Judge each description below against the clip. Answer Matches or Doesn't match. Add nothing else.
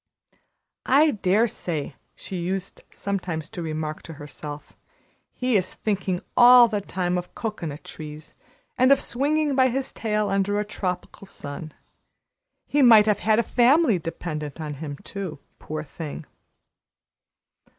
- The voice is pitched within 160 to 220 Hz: Matches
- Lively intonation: Matches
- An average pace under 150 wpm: Matches